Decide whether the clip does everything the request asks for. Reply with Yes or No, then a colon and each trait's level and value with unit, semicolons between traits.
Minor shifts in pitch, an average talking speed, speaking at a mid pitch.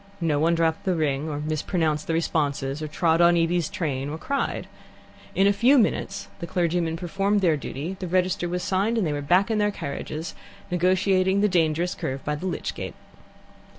No: average, 3.4 semitones; average, 190 wpm; medium, 170 Hz